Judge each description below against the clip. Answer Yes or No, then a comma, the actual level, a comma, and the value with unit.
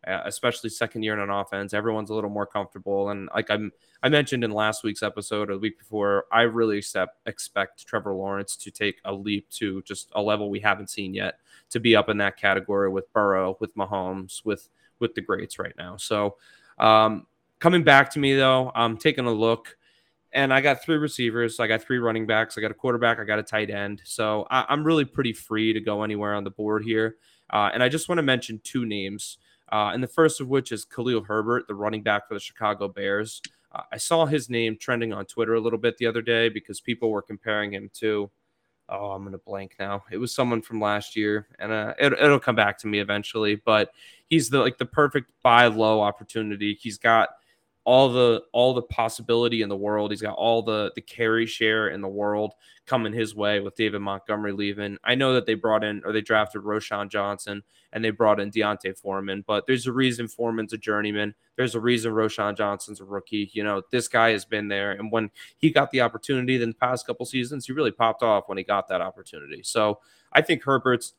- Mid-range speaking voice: No, low, 110 Hz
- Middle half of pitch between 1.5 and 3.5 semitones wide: Yes, narrow, 2.5 semitones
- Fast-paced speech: Yes, fast, 225 wpm